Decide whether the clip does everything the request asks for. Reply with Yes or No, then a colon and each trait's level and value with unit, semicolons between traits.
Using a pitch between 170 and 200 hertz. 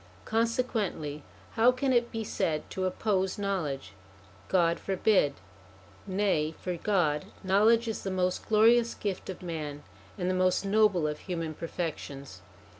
Yes: medium, 185 Hz